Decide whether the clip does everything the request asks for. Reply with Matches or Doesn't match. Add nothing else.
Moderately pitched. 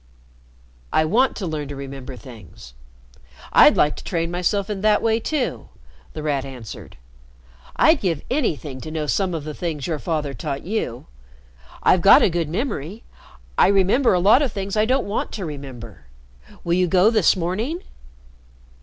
Matches